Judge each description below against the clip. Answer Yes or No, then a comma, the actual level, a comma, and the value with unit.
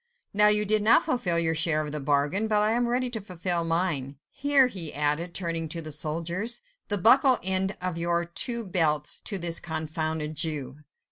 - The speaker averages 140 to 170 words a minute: No, average, 190 wpm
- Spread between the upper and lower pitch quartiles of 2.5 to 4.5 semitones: No, average, 4.9 semitones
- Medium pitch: Yes, medium, 170 Hz